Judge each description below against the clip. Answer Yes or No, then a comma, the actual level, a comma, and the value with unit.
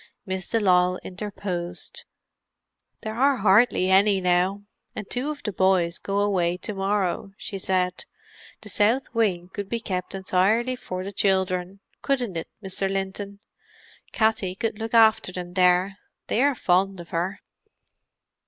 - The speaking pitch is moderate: No, high, 195 Hz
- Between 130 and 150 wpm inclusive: Yes, average, 140 wpm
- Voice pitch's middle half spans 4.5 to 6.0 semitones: No, narrow, 2.6 semitones